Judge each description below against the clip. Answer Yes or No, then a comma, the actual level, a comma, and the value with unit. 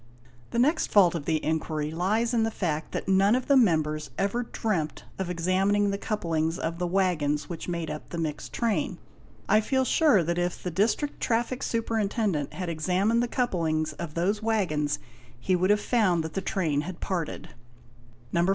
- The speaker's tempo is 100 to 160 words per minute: No, average, 185 wpm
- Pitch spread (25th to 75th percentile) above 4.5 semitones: Yes, average, 5.1 semitones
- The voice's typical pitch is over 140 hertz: Yes, medium, 185 Hz